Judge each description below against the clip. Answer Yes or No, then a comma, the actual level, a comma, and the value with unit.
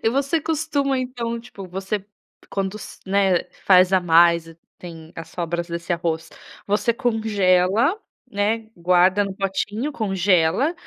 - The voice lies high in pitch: Yes, high, 195 Hz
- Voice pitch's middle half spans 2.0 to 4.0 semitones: No, average, 4.7 semitones